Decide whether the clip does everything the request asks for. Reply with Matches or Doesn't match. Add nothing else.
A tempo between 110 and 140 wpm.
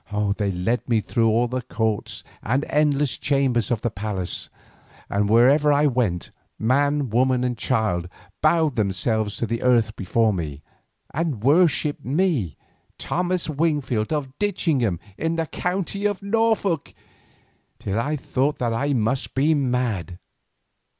Matches